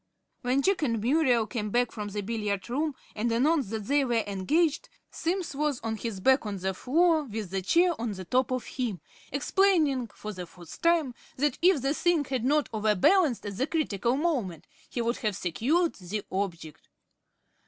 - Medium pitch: No, high, 245 Hz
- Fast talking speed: No, average, 185 wpm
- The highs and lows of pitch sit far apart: Yes, wide, 6.4 semitones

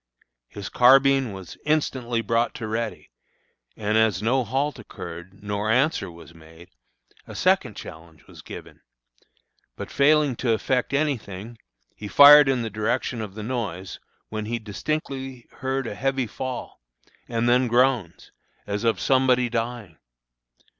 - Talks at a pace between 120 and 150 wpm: Yes, average, 145 wpm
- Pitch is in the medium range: No, low, 115 Hz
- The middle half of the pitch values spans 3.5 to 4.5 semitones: Yes, average, 4.2 semitones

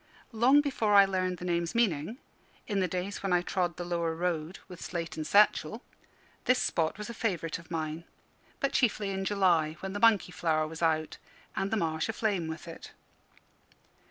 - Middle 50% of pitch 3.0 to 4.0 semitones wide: Yes, average, 3.7 semitones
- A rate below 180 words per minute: No, average, 185 wpm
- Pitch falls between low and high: Yes, medium, 180 Hz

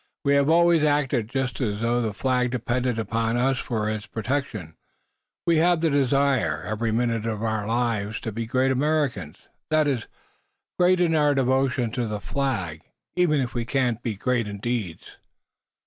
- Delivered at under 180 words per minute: Yes, average, 170 wpm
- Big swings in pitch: No, average, 4.1 semitones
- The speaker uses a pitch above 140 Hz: No, low, 125 Hz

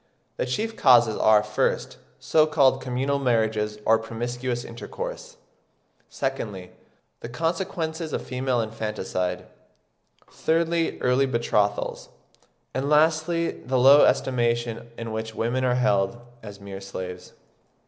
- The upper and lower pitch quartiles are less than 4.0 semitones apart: No, average, 4.3 semitones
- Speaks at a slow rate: Yes, slow, 115 wpm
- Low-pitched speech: Yes, low, 125 Hz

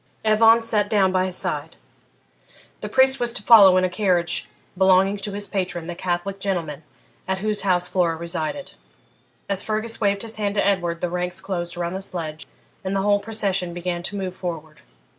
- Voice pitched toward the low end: No, high, 190 Hz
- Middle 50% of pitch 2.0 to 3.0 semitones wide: Yes, average, 2.7 semitones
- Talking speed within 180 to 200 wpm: Yes, average, 185 wpm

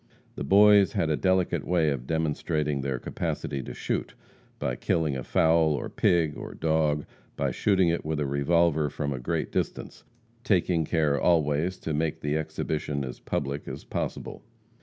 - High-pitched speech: No, very low, 80 Hz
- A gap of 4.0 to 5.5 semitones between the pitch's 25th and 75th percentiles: No, average, 2.8 semitones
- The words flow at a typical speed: Yes, average, 165 wpm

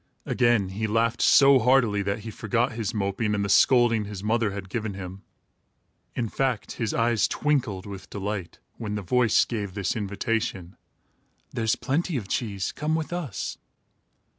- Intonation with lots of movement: No, average, 3.1 semitones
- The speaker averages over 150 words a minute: Yes, average, 160 wpm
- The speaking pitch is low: Yes, low, 110 Hz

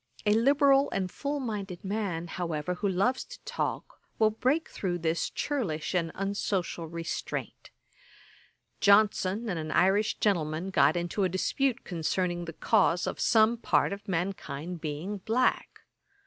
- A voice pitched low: No, high, 190 Hz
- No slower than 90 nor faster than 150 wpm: Yes, average, 140 wpm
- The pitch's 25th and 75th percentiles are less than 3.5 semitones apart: No, average, 4.1 semitones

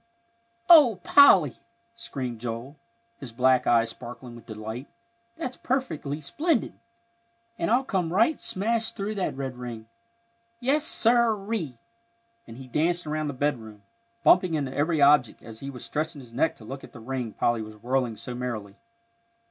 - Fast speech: No, average, 155 wpm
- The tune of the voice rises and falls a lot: Yes, wide, 8.6 semitones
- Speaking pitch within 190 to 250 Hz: No, medium, 140 Hz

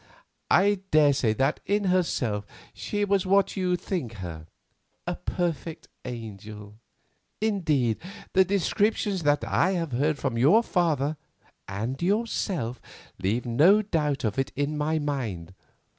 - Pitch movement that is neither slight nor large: No, wide, 8.1 semitones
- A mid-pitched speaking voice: Yes, medium, 150 Hz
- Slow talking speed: Yes, slow, 130 wpm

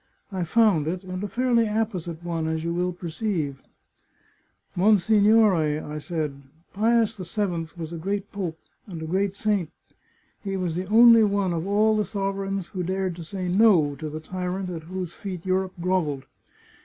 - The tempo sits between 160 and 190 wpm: Yes, average, 180 wpm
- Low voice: No, medium, 185 Hz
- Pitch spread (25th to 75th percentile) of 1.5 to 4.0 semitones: Yes, average, 3.5 semitones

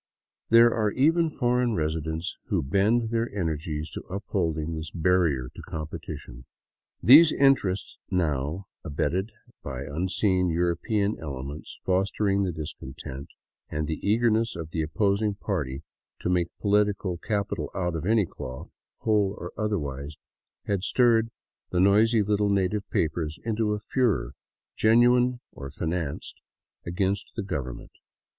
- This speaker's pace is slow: Yes, slow, 130 wpm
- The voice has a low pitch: Yes, very low, 95 Hz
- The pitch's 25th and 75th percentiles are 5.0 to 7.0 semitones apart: Yes, average, 5.3 semitones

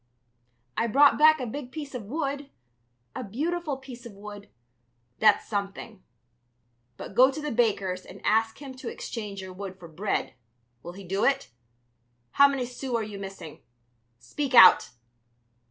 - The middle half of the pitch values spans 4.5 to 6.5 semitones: Yes, wide, 5.6 semitones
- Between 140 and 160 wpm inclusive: Yes, average, 155 wpm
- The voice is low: No, high, 230 Hz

